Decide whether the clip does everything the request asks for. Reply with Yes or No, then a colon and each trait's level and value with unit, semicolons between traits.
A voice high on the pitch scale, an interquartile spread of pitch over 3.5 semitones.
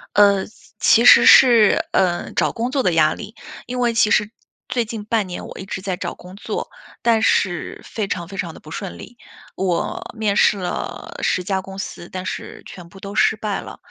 No: high, 200 Hz; average, 3.2 semitones